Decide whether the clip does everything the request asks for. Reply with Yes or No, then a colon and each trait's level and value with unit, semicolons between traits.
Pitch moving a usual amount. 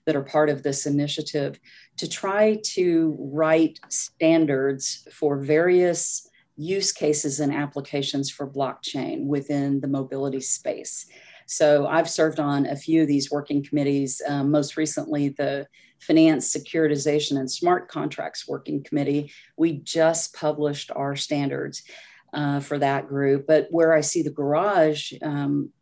No: narrow, 2.1 semitones